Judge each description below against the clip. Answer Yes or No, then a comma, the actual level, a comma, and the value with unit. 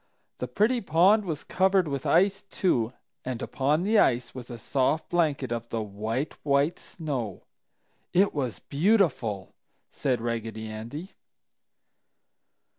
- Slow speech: Yes, slow, 125 wpm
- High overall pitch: No, medium, 140 Hz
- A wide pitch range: Yes, wide, 7.1 semitones